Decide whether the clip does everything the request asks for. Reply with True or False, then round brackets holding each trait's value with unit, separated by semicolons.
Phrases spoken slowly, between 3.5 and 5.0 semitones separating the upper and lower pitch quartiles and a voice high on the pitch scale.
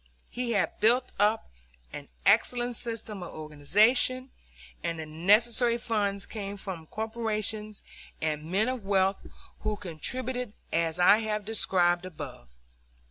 True (125 wpm; 4.4 semitones; 210 Hz)